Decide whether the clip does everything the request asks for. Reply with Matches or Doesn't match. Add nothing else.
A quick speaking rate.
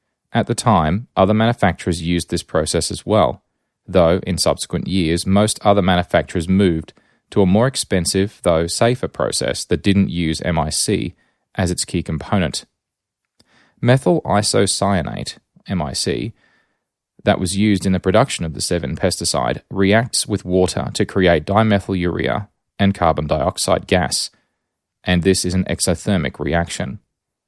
Doesn't match